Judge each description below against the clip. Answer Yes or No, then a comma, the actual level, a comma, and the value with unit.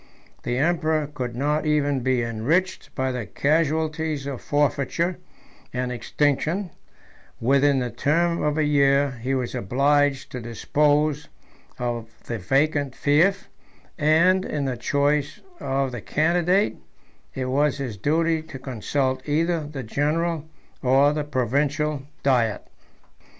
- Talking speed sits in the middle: No, slow, 125 wpm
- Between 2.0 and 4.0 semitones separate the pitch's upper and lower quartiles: Yes, average, 3.0 semitones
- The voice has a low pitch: No, medium, 145 Hz